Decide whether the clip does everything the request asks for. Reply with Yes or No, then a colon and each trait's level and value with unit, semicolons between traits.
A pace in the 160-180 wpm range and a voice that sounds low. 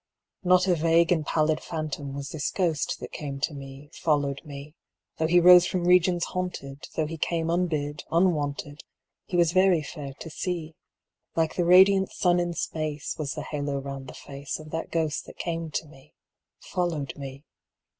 No: average, 175 wpm; medium, 160 Hz